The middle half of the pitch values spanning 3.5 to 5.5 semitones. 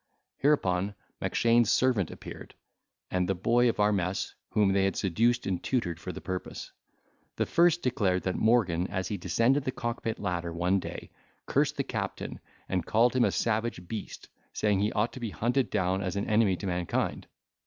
Yes: average, 4.3 semitones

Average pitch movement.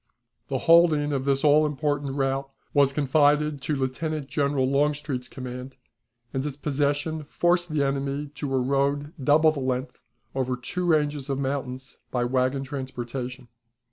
No: narrow, 2.0 semitones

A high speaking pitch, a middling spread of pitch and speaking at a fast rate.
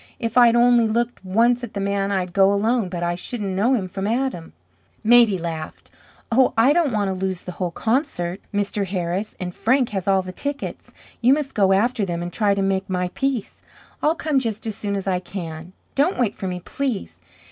Yes: high, 200 Hz; average, 4.4 semitones; fast, 210 wpm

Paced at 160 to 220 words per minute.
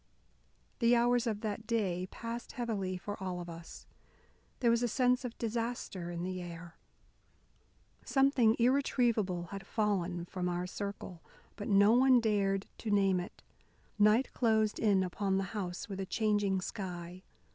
No: average, 150 wpm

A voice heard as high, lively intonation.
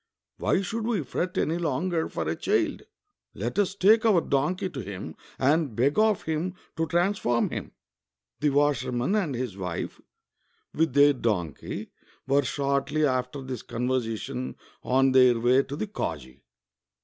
No: medium, 140 Hz; wide, 5.8 semitones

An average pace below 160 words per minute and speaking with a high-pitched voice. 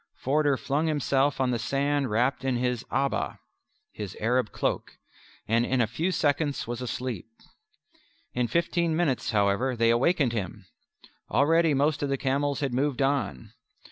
No: average, 150 wpm; low, 135 Hz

